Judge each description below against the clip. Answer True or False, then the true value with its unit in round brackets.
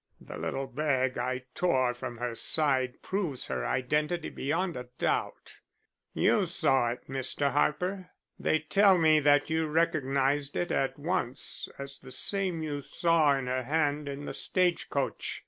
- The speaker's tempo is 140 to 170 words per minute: True (155 wpm)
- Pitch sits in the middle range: True (145 Hz)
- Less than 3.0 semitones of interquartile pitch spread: False (3.6 semitones)